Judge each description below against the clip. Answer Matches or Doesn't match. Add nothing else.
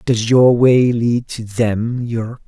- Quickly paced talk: Doesn't match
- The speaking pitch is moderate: Doesn't match